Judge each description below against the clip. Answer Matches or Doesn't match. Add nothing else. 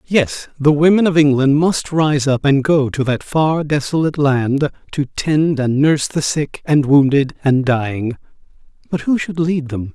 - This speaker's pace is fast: Doesn't match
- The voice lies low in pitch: Doesn't match